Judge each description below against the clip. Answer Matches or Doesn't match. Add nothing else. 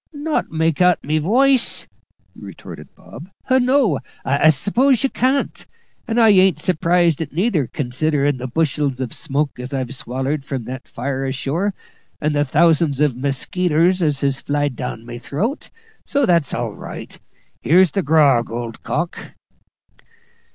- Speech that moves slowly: Doesn't match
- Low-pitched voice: Doesn't match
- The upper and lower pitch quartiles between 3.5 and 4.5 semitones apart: Doesn't match